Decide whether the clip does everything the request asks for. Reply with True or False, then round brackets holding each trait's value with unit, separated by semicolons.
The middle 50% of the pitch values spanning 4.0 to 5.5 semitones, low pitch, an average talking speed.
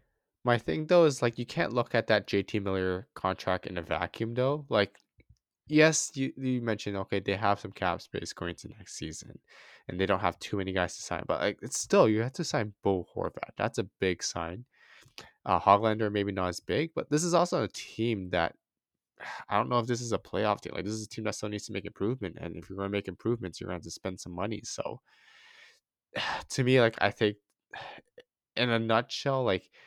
False (4.4 semitones; 105 Hz; 225 wpm)